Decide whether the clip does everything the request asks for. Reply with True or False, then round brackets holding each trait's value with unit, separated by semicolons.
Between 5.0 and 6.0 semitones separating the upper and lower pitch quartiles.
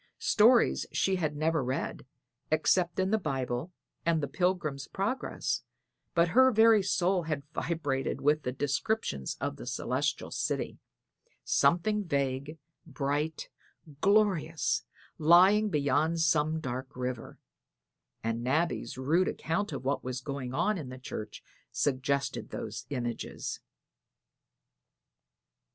True (5.3 semitones)